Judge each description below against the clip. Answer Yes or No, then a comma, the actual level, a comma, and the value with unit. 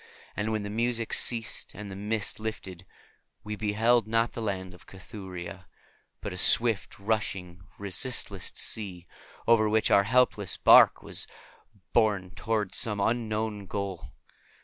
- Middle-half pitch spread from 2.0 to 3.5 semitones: Yes, average, 2.8 semitones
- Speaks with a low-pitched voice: Yes, low, 105 Hz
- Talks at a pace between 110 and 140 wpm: Yes, slow, 135 wpm